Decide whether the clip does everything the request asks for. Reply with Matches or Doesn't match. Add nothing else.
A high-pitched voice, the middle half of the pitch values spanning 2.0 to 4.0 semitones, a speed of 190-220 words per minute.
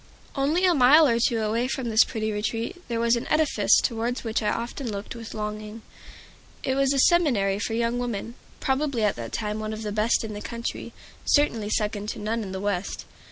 Matches